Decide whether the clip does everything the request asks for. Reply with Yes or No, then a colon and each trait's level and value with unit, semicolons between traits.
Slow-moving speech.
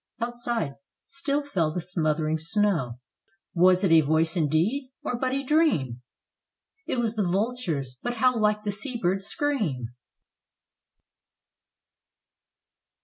Yes: slow, 120 wpm